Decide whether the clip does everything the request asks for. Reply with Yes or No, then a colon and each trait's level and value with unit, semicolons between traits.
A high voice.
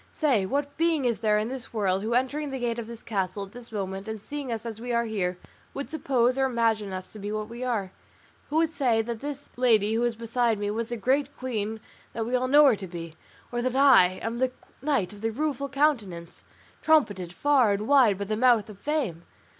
Yes: high, 235 Hz